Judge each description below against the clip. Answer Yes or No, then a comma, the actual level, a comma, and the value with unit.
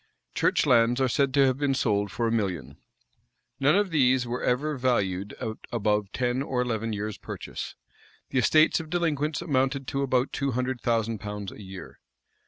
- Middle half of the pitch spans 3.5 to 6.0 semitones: Yes, average, 4.2 semitones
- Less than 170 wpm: No, average, 180 wpm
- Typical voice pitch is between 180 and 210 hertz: No, low, 125 Hz